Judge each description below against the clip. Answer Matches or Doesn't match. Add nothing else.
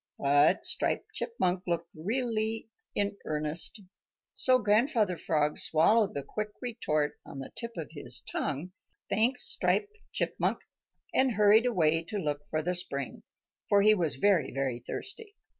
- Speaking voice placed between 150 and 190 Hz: Matches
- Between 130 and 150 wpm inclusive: Matches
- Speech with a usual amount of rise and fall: Doesn't match